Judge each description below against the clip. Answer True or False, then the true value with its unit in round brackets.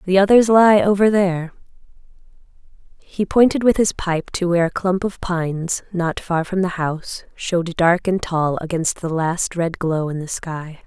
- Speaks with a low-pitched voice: False (180 Hz)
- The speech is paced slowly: False (180 wpm)